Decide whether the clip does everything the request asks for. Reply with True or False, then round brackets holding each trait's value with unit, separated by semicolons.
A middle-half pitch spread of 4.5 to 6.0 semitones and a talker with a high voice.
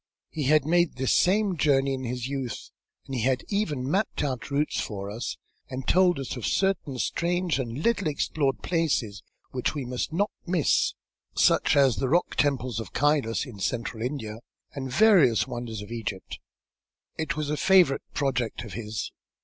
False (4.9 semitones; 135 Hz)